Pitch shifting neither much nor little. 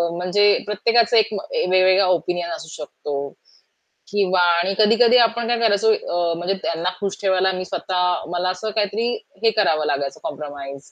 Yes: average, 3.4 semitones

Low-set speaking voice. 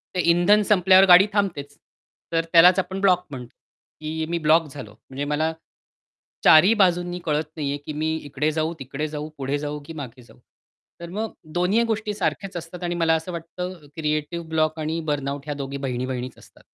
No: medium, 160 Hz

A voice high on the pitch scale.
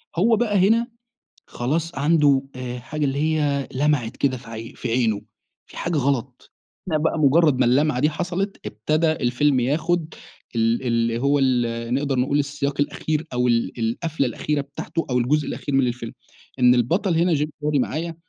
No: medium, 140 Hz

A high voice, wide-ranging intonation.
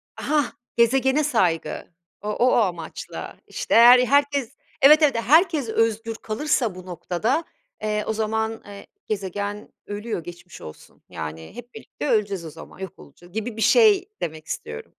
Yes: high, 220 Hz; wide, 5.9 semitones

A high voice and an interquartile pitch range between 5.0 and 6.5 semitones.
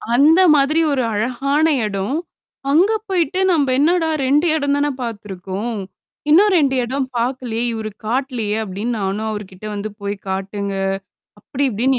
Yes: high, 245 Hz; wide, 5.6 semitones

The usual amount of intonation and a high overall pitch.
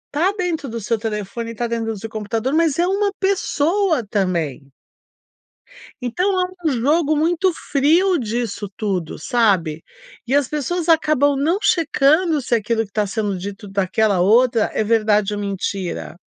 No: wide, 7.0 semitones; high, 235 Hz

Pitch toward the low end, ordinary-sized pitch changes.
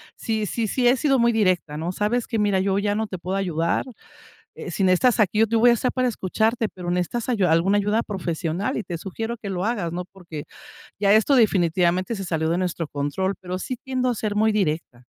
No: high, 200 Hz; average, 4.1 semitones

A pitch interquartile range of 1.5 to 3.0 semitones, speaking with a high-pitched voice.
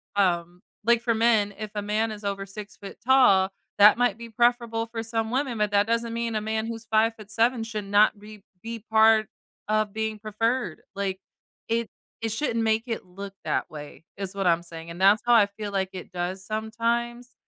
Yes: narrow, 2.4 semitones; high, 220 Hz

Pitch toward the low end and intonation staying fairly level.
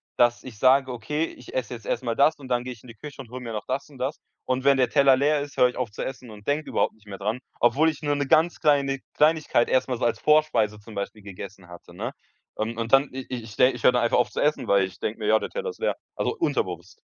No: low, 125 Hz; average, 4.0 semitones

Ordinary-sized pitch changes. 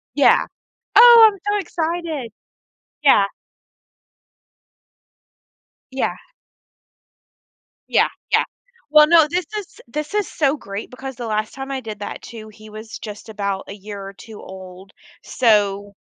No: wide, 6.9 semitones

